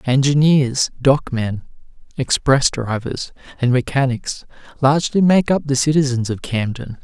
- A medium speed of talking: No, slow, 110 wpm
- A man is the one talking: Yes, male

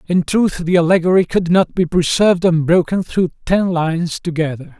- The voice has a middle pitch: Yes, medium, 175 Hz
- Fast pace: No, average, 165 wpm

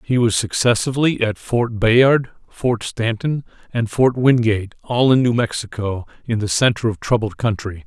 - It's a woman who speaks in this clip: No, male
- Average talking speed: Yes, average, 160 wpm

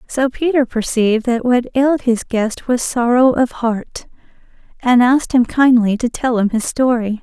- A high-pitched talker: Yes, high, 245 Hz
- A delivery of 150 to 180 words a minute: Yes, average, 175 wpm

